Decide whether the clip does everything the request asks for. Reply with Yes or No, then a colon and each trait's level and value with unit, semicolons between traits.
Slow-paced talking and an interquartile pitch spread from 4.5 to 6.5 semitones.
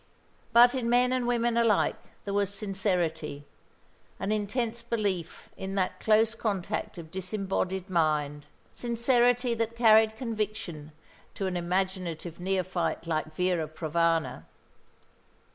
Yes: slow, 115 wpm; average, 5.0 semitones